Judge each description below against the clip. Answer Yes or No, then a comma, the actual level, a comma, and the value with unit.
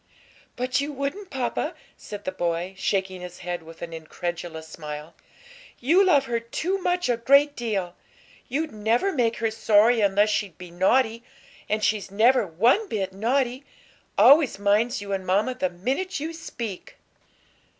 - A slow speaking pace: No, average, 155 wpm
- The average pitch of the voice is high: Yes, high, 220 Hz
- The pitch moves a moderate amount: No, wide, 6.0 semitones